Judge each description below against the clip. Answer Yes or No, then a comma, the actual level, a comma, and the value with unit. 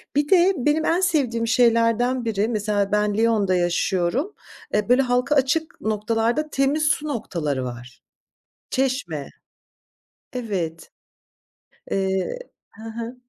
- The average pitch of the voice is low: No, high, 230 Hz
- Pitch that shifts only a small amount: No, average, 5.2 semitones